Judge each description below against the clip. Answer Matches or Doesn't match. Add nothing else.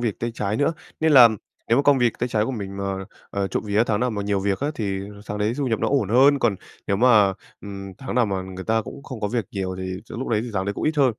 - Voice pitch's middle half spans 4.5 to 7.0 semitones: Doesn't match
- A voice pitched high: Doesn't match